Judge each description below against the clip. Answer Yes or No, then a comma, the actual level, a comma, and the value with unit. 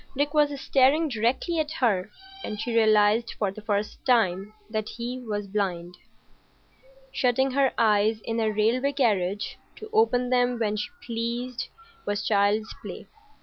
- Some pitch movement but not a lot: Yes, average, 3.5 semitones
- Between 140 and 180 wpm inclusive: Yes, average, 150 wpm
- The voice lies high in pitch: Yes, high, 230 Hz